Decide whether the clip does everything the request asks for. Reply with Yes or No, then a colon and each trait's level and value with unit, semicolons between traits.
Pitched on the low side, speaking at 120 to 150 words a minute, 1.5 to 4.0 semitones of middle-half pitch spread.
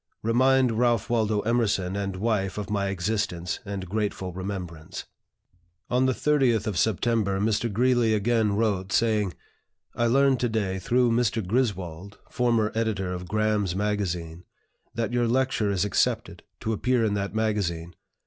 Yes: low, 105 Hz; average, 145 wpm; average, 3.3 semitones